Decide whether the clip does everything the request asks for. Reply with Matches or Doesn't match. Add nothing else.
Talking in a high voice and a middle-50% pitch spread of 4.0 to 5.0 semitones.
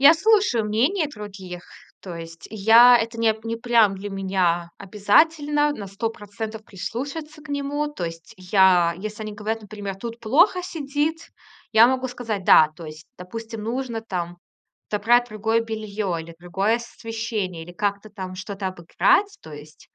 Matches